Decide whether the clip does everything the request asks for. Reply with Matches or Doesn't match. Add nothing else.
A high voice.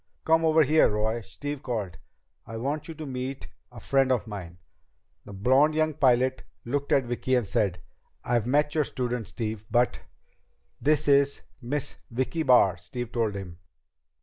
Doesn't match